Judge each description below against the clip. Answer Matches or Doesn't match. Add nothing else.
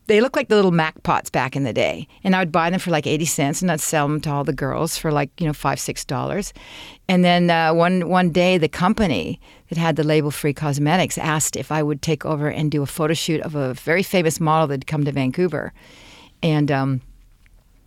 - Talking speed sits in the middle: Doesn't match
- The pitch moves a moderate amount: Matches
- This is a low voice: Doesn't match